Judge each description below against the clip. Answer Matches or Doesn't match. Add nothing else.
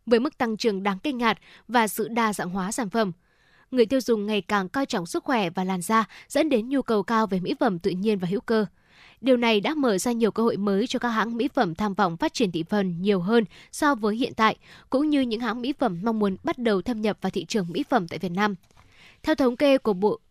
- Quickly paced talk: Matches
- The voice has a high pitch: Matches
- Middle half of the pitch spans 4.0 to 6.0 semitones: Doesn't match